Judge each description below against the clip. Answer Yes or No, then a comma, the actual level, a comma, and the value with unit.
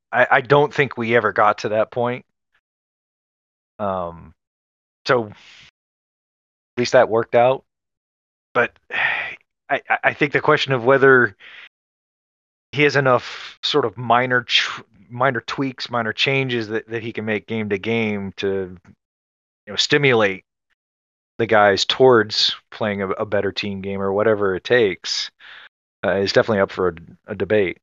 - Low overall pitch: Yes, low, 110 Hz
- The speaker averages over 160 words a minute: No, average, 150 wpm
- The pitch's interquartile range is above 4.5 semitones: Yes, average, 5.1 semitones